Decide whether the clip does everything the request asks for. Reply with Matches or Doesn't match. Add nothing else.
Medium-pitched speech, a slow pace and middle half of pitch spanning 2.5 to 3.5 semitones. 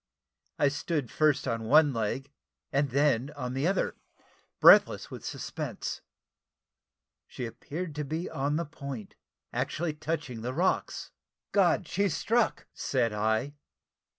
Doesn't match